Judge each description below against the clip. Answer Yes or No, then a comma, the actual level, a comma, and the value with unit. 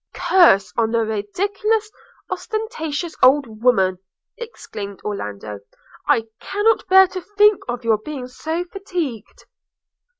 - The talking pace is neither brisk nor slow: No, slow, 110 wpm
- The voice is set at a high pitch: Yes, very high, 290 Hz